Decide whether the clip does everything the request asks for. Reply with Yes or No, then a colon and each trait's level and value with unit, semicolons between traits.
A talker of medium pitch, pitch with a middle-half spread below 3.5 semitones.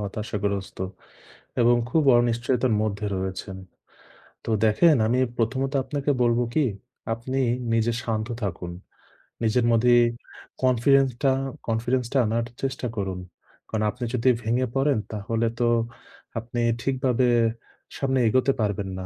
No: low, 120 Hz; average, 3.1 semitones